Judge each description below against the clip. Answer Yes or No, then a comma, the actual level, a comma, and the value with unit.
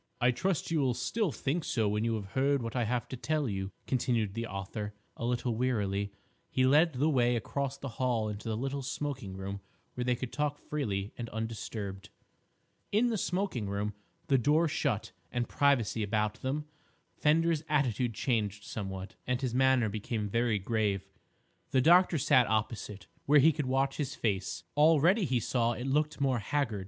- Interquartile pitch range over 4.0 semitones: Yes, average, 4.8 semitones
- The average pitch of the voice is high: No, low, 125 Hz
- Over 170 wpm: Yes, average, 180 wpm